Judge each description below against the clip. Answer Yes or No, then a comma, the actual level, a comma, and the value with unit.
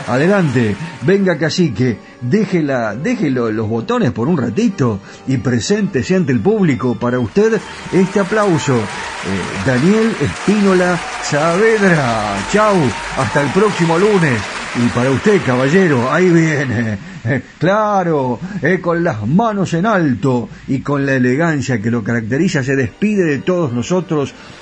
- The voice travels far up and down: Yes, wide, 7.1 semitones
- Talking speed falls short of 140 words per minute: Yes, average, 130 wpm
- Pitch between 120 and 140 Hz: No, medium, 155 Hz